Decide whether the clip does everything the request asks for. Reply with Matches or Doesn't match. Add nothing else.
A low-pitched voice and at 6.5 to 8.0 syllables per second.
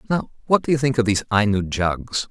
Doesn't match